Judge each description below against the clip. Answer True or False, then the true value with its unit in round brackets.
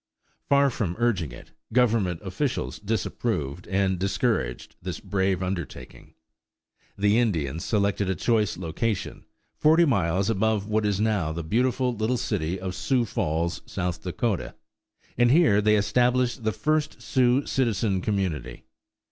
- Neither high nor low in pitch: False (105 Hz)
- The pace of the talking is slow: True (130 wpm)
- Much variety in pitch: False (4.6 semitones)